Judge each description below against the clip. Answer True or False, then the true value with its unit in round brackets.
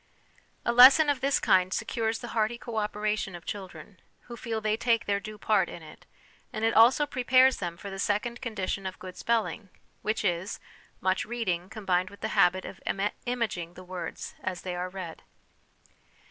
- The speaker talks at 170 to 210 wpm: True (180 wpm)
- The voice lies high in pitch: True (210 Hz)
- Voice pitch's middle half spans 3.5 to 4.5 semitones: True (4.0 semitones)